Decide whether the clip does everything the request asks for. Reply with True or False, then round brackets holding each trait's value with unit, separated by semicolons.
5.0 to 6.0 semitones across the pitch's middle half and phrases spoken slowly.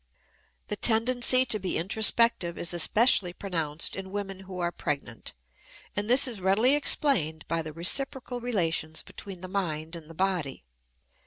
False (5.4 semitones; 150 wpm)